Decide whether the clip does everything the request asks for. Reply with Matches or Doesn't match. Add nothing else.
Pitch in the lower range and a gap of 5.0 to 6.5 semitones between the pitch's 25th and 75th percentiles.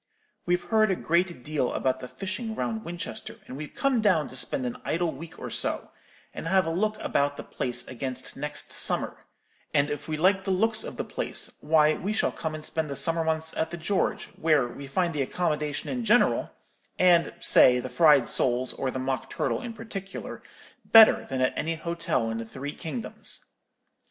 Doesn't match